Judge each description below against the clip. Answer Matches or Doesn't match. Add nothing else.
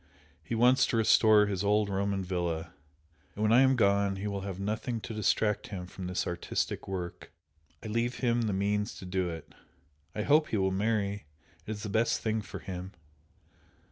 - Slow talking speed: Doesn't match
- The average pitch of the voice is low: Matches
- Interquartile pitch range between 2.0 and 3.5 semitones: Matches